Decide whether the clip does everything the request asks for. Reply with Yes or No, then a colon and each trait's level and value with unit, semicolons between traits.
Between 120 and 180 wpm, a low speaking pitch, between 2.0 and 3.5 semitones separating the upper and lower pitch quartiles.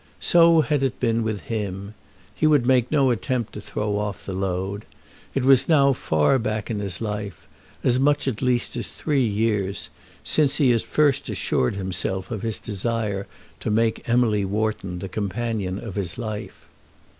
No: average, 170 wpm; low, 110 Hz; average, 4.1 semitones